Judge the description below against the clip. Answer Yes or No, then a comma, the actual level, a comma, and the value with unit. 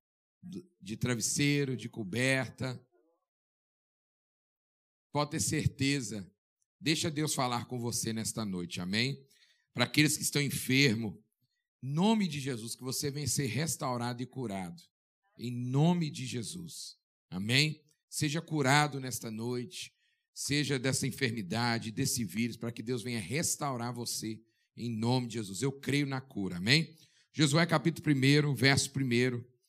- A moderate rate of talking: Yes, average, 130 wpm